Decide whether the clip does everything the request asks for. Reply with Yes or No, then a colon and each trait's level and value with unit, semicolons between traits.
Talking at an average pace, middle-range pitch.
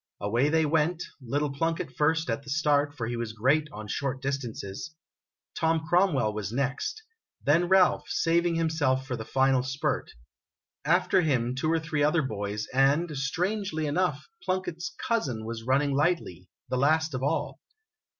Yes: average, 155 wpm; medium, 145 Hz